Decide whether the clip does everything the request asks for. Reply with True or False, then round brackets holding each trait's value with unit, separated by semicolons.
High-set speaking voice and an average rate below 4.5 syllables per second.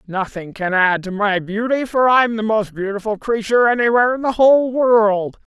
False (220 Hz; 5.1 syllables/s)